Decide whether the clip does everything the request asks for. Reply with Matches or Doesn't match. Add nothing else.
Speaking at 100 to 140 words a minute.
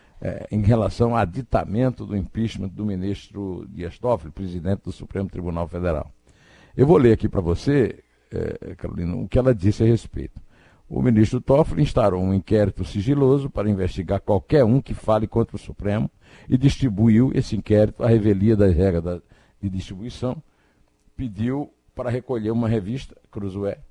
Doesn't match